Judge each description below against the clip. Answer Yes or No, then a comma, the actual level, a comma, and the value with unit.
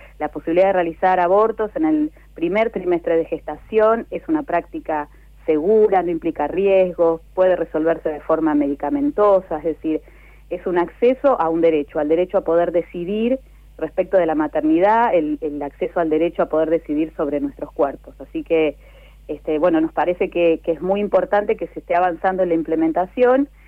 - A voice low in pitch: No, medium, 170 Hz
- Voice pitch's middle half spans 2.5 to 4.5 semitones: Yes, average, 3.5 semitones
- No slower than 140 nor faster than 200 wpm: Yes, average, 175 wpm